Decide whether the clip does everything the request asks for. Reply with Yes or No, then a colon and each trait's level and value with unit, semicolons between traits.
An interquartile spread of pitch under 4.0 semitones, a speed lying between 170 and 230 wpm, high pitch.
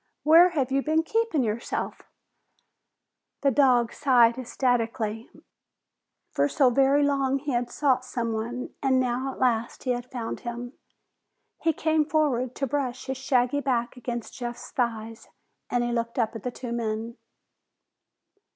No: narrow, 2.6 semitones; average, 145 wpm; very high, 250 Hz